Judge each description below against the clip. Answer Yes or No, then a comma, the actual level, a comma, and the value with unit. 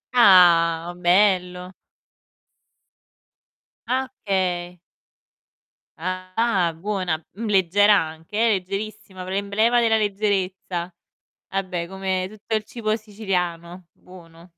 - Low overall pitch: No, high, 190 Hz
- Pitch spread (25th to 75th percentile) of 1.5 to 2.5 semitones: No, average, 2.9 semitones